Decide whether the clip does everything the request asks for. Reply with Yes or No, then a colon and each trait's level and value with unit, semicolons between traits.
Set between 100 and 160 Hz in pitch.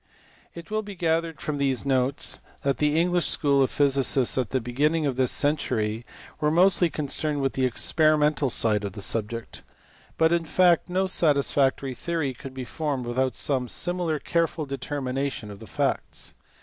Yes: medium, 140 Hz